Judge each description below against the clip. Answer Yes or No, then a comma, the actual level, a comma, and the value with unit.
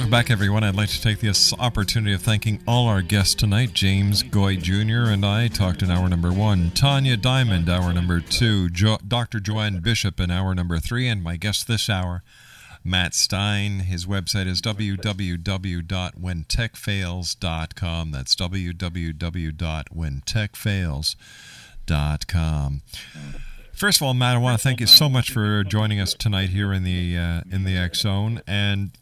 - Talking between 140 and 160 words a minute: Yes, average, 155 wpm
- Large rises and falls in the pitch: No, average, 3.7 semitones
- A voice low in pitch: Yes, low, 100 Hz